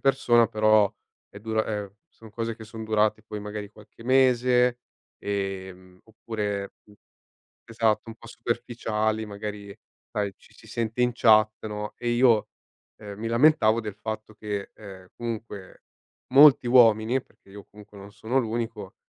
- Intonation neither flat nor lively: No, narrow, 2.0 semitones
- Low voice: Yes, low, 110 Hz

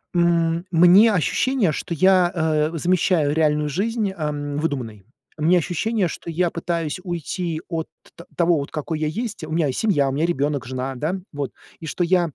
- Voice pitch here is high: No, medium, 165 Hz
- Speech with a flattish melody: No, average, 3.0 semitones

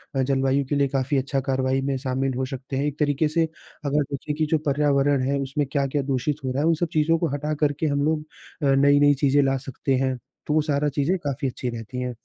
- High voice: No, medium, 140 Hz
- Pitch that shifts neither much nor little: No, narrow, 1.8 semitones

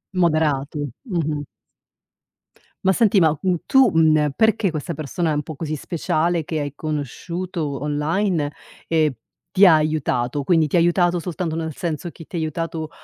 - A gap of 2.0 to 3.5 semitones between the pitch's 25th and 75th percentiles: Yes, average, 2.7 semitones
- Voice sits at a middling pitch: Yes, medium, 160 Hz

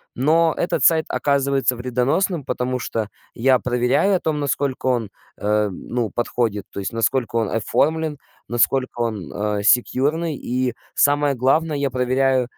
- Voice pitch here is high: No, low, 130 Hz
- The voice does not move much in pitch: No, average, 3.4 semitones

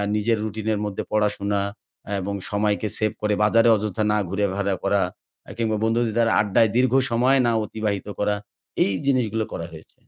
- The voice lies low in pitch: Yes, low, 105 Hz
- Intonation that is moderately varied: No, narrow, 1.9 semitones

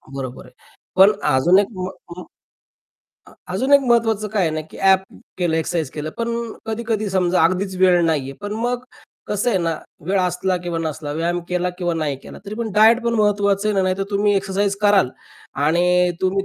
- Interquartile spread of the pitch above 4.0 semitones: No, average, 3.1 semitones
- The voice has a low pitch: No, high, 190 Hz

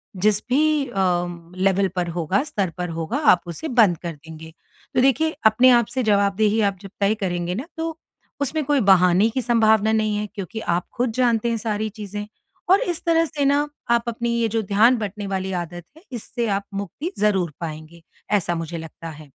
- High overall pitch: Yes, high, 210 Hz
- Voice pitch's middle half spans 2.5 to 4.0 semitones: No, average, 5.1 semitones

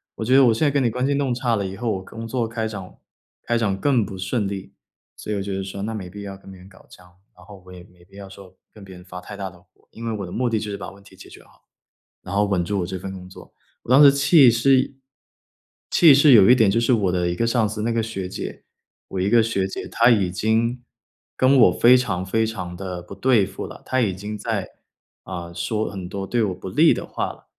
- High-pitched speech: No, low, 105 Hz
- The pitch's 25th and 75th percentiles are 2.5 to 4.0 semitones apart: Yes, average, 3.7 semitones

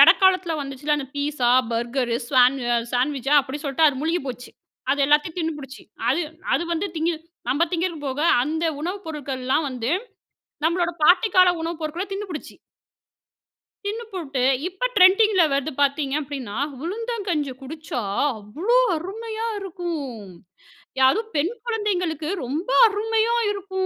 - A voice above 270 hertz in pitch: Yes, very high, 315 Hz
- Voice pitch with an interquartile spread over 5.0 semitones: Yes, wide, 5.4 semitones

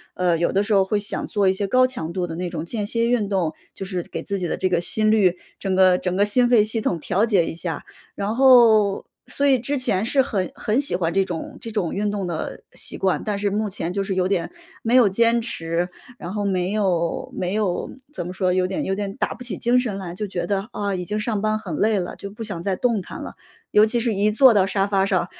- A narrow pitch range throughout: No, average, 3.0 semitones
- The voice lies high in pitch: Yes, high, 200 Hz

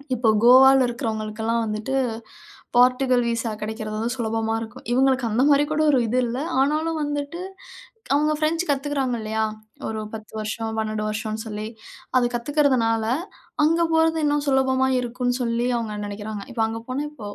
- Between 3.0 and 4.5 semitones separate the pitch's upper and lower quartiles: Yes, average, 3.6 semitones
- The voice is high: Yes, high, 240 Hz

